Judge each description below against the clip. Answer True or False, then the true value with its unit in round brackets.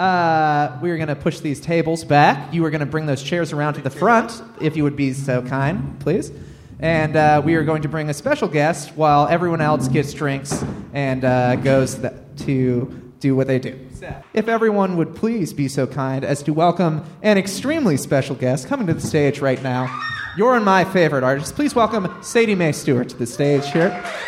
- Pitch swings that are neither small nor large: True (4.2 semitones)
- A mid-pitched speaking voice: True (150 Hz)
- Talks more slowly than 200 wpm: False (205 wpm)